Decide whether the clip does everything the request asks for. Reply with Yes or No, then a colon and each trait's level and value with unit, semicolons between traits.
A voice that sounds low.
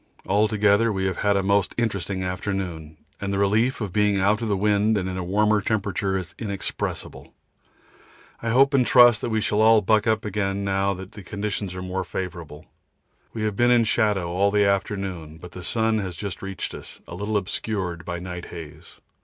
Yes: low, 100 Hz